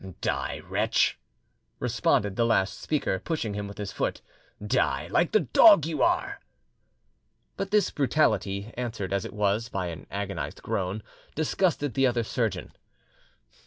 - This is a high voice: No, low, 115 Hz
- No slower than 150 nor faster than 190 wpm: No, average, 140 wpm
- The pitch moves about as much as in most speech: No, wide, 6.7 semitones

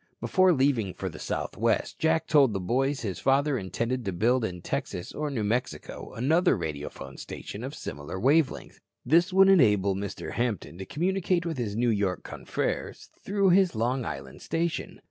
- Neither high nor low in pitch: No, low, 125 Hz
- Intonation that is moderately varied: No, wide, 8.2 semitones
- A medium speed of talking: Yes, average, 170 wpm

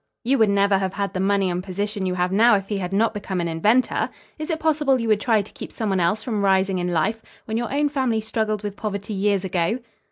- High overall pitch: Yes, high, 205 Hz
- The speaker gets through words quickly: Yes, fast, 255 wpm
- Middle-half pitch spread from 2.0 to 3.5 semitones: Yes, average, 2.8 semitones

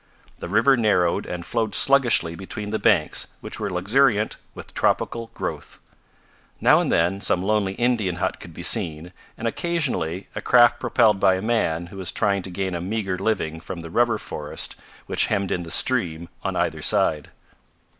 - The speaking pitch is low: Yes, very low, 95 Hz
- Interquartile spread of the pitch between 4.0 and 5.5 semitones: Yes, average, 4.7 semitones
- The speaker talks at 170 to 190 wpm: Yes, average, 175 wpm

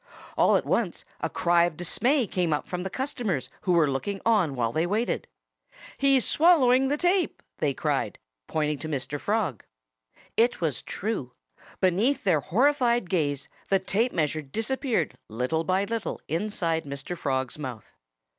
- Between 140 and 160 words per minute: Yes, average, 150 wpm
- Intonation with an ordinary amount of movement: No, wide, 7.6 semitones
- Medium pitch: Yes, medium, 180 Hz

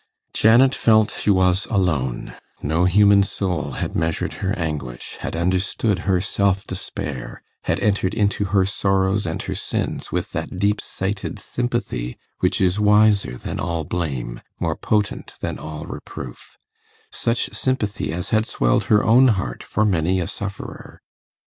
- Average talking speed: Yes, average, 150 wpm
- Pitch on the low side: Yes, very low, 95 Hz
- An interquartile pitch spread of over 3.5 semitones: Yes, average, 4.0 semitones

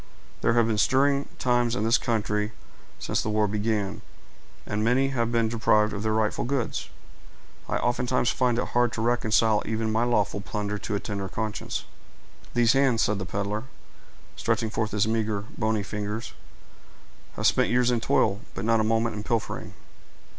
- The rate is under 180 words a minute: Yes, average, 170 wpm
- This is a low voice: Yes, low, 110 Hz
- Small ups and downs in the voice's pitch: Yes, narrow, 2.1 semitones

